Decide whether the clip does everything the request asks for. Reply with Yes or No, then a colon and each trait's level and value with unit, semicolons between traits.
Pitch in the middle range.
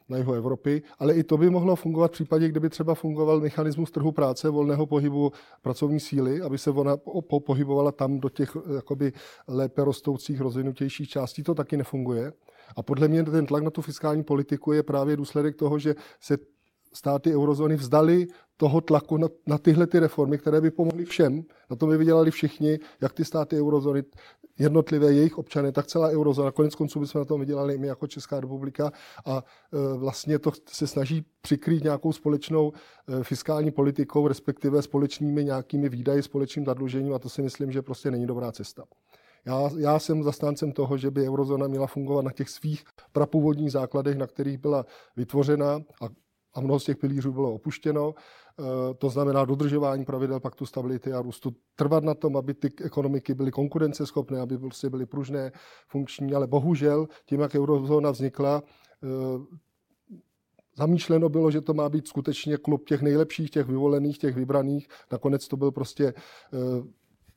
Yes: medium, 145 Hz